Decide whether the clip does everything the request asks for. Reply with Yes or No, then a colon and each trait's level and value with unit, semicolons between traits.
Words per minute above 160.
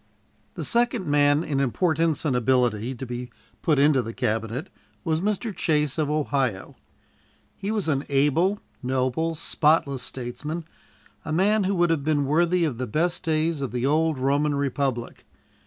No: average, 155 wpm